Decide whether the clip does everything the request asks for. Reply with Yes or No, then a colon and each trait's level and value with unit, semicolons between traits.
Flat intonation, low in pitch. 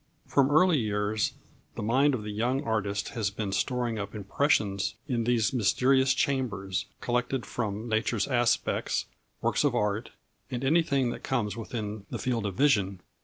No: average, 4.0 semitones; low, 115 Hz